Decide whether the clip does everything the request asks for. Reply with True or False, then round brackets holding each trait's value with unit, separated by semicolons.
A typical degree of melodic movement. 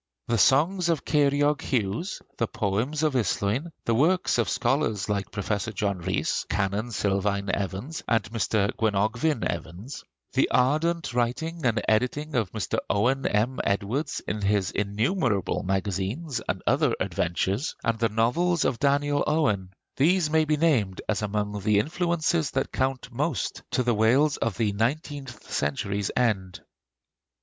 False (6.2 semitones)